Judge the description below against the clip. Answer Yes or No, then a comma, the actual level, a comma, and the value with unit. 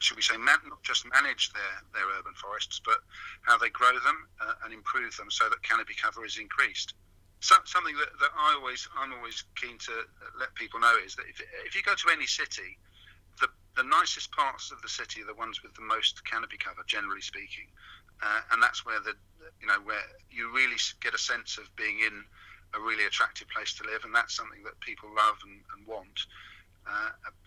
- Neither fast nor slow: No, fast, 210 wpm